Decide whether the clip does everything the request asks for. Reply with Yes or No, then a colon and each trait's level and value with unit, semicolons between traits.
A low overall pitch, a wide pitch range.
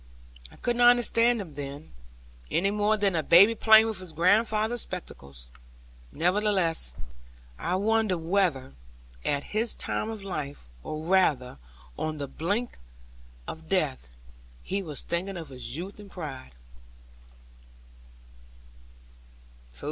No: medium, 185 Hz; wide, 5.7 semitones